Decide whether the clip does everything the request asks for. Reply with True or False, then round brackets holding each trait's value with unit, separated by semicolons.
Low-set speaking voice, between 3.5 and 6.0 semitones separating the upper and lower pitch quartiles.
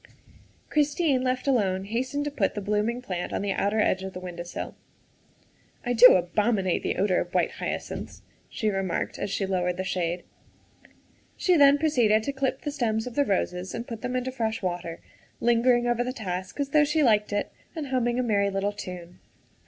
False (220 Hz; 5.1 semitones)